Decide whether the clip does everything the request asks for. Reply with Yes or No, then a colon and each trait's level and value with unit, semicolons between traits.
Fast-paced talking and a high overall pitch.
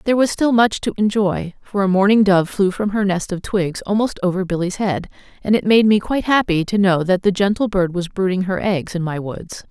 Yes: fast, 240 wpm; high, 195 Hz